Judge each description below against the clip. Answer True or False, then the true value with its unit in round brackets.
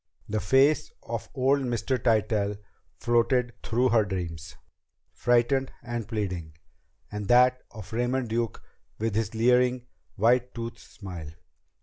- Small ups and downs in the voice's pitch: False (3.1 semitones)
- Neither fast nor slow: False (120 wpm)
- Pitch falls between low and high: False (115 Hz)